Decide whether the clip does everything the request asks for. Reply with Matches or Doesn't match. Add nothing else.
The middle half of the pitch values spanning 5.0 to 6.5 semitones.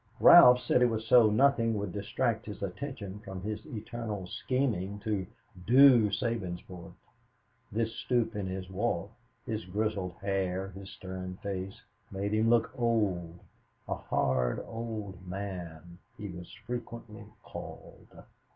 Doesn't match